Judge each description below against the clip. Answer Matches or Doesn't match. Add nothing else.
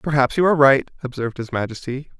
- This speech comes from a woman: Doesn't match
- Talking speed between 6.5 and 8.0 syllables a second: Matches